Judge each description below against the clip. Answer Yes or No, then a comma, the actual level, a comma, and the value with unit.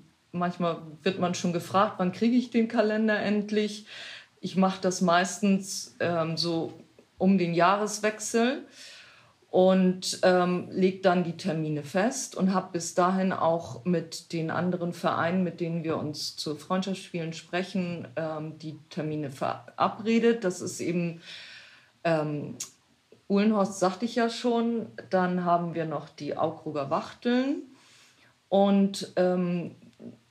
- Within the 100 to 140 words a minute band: Yes, average, 130 wpm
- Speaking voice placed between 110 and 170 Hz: No, medium, 180 Hz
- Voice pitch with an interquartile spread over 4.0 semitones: No, average, 3.4 semitones